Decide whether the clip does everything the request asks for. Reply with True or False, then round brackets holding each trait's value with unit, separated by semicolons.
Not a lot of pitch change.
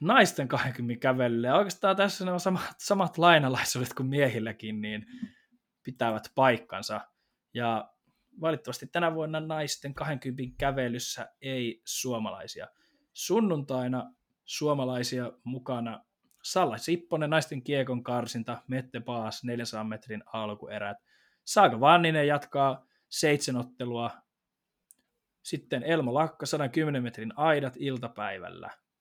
False (4.9 semitones)